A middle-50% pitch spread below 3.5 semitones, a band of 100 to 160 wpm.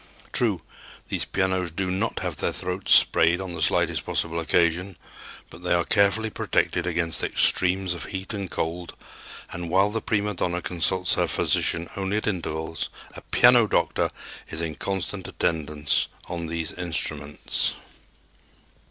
Yes: narrow, 2.5 semitones; average, 145 wpm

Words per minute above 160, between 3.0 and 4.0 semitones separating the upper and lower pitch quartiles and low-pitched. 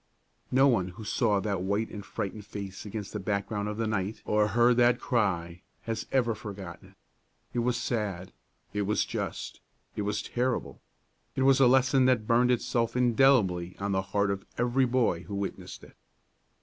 Yes: average, 175 wpm; average, 3.6 semitones; low, 105 Hz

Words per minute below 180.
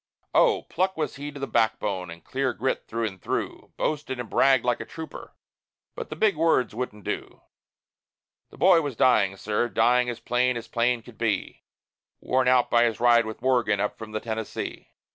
No: average, 190 wpm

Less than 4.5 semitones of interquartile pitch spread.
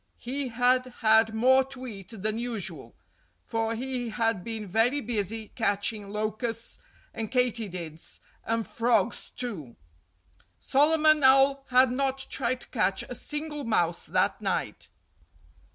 Yes: average, 3.1 semitones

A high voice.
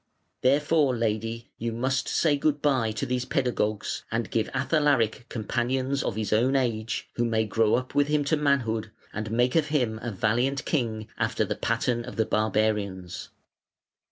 No: low, 120 Hz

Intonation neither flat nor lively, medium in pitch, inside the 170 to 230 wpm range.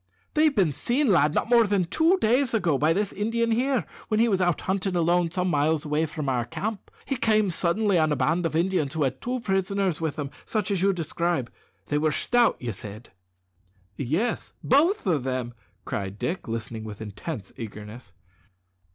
No: wide, 6.9 semitones; medium, 175 Hz; average, 185 wpm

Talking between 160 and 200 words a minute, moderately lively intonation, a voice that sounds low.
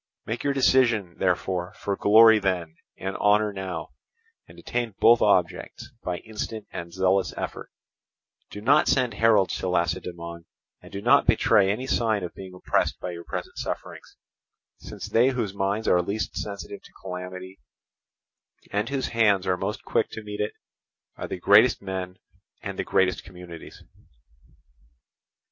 No: average, 150 wpm; average, 3.4 semitones; low, 100 Hz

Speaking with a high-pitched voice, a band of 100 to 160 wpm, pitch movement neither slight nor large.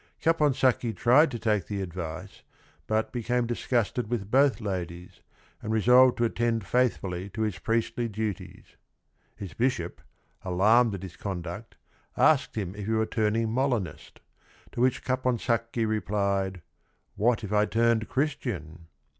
No: low, 110 Hz; average, 140 wpm; average, 3.7 semitones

